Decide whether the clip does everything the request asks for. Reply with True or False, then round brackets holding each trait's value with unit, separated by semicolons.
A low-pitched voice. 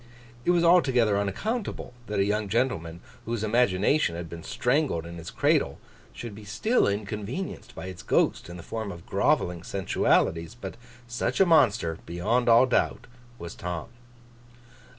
True (105 Hz)